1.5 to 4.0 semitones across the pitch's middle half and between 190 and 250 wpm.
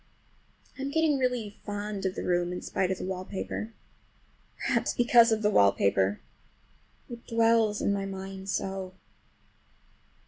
No: average, 3.5 semitones; slow, 135 wpm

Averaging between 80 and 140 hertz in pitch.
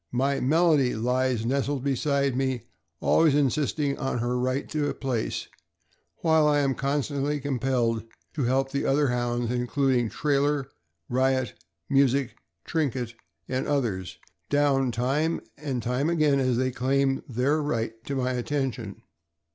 Yes: low, 135 Hz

